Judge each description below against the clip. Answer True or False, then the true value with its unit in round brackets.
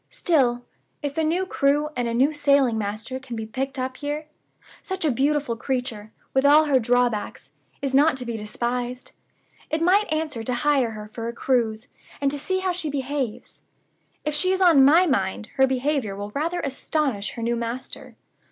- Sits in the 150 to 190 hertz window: False (265 Hz)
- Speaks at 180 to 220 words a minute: True (185 wpm)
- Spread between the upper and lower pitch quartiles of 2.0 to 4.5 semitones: True (4.1 semitones)